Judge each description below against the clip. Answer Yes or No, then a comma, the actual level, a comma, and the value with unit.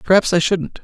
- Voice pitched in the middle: Yes, medium, 180 Hz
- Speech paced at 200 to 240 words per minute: Yes, fast, 215 wpm